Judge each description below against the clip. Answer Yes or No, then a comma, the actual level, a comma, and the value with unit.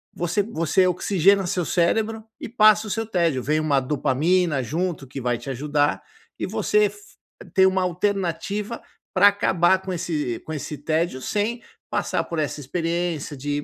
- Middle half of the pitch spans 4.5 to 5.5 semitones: Yes, average, 5.1 semitones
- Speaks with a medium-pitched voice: Yes, medium, 175 Hz